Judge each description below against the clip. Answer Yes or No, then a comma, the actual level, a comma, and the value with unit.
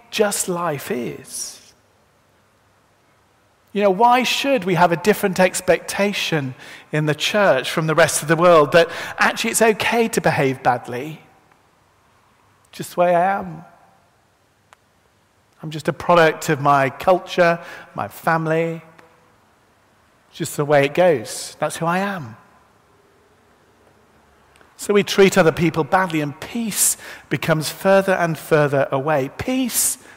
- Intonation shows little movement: No, average, 4.5 semitones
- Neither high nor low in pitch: Yes, medium, 165 Hz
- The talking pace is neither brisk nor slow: No, slow, 130 wpm